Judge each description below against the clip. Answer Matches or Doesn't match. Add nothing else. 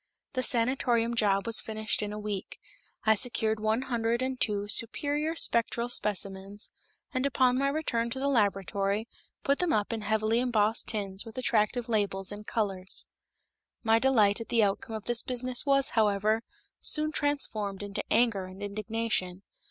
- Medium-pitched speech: Doesn't match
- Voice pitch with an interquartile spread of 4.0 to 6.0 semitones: Doesn't match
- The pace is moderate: Matches